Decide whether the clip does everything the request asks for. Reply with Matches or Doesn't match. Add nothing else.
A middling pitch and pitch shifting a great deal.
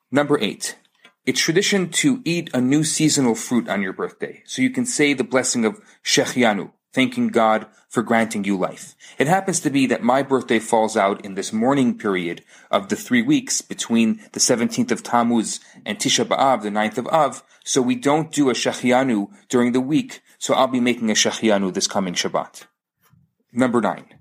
Doesn't match